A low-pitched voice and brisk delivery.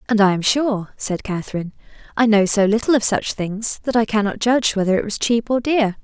No: high, 215 Hz; fast, 230 wpm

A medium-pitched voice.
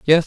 Yes: medium, 160 Hz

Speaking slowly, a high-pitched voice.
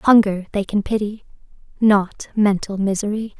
Yes: slow, 105 wpm; high, 205 Hz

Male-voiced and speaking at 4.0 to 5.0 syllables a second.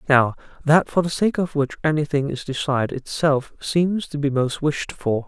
Yes: male; 4.8 syllables/s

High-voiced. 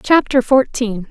Yes: high, 245 Hz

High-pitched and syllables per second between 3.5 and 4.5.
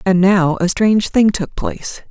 No: high, 195 Hz; 4.7 syllables/s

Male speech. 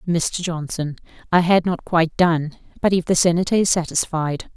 No: female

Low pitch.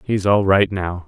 Yes: very low, 95 Hz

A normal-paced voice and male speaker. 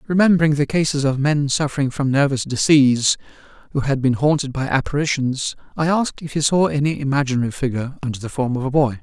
Yes: average, 195 wpm; male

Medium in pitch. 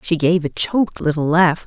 Yes: medium, 165 Hz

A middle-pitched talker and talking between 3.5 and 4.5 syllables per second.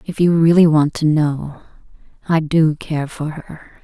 Yes: medium, 155 Hz; 4.0 syllables/s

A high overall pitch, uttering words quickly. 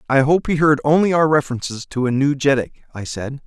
No: medium, 140 Hz; fast, 225 wpm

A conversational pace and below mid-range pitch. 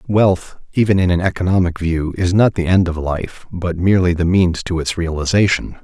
Yes: average, 195 wpm; very low, 90 Hz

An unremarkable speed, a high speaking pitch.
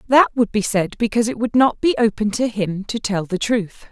No: fast, 245 wpm; high, 220 Hz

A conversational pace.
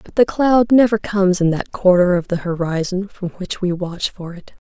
No: fast, 220 wpm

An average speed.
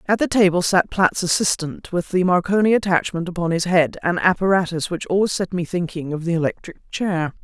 Yes: average, 185 wpm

